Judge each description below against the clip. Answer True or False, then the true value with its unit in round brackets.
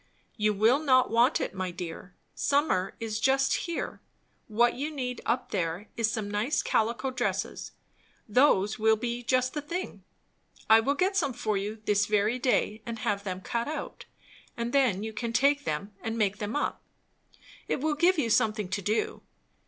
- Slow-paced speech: False (175 wpm)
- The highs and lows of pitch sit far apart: False (4.3 semitones)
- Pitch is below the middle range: False (230 Hz)